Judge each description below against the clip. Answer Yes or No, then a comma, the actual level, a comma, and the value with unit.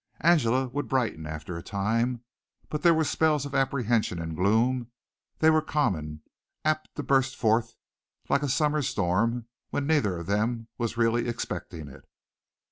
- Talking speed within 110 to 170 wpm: Yes, average, 155 wpm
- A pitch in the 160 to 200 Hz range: No, low, 120 Hz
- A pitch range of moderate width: No, wide, 6.0 semitones